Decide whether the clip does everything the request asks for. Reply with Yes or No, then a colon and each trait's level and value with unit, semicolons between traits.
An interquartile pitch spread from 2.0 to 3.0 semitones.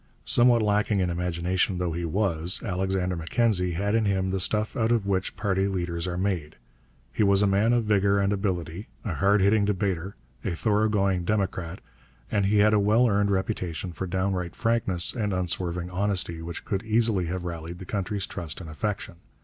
Yes: average, 2.7 semitones